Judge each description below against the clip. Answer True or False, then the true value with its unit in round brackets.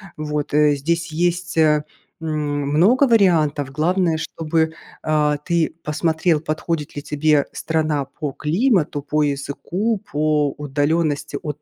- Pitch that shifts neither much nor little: False (2.2 semitones)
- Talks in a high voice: False (155 Hz)